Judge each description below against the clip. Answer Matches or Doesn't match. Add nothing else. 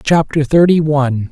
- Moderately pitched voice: Matches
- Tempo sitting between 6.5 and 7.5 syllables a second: Doesn't match